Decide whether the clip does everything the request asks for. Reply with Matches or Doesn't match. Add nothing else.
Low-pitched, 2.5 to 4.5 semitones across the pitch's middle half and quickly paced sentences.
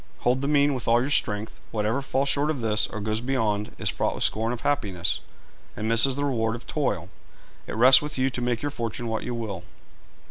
Matches